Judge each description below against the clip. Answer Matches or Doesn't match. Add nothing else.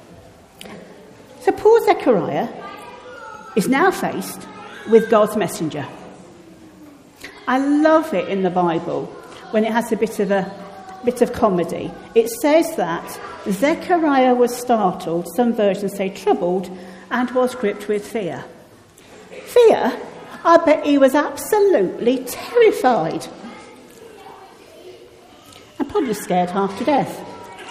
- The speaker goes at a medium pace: Doesn't match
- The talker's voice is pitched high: Matches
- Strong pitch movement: Matches